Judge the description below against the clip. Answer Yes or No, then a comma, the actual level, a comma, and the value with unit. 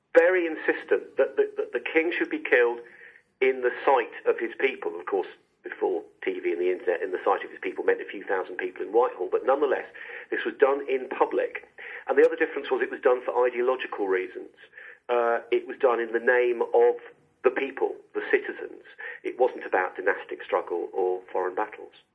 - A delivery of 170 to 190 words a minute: No, average, 200 wpm